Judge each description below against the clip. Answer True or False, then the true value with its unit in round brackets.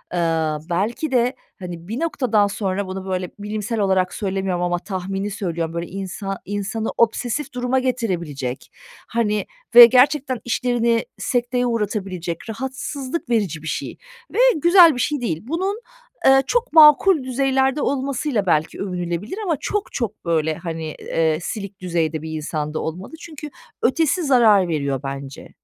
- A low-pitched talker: False (210 Hz)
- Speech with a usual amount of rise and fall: False (6.8 semitones)